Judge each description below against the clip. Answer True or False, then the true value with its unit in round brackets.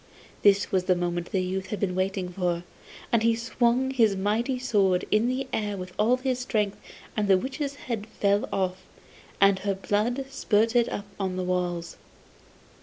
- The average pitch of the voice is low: False (205 Hz)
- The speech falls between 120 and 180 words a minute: True (170 wpm)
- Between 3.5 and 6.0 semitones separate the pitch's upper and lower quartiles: True (4.0 semitones)